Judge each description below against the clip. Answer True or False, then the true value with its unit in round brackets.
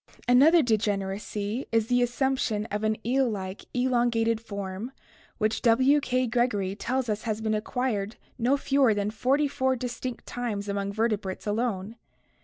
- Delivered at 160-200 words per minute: False (145 wpm)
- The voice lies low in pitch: False (230 Hz)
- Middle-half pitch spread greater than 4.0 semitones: False (3.3 semitones)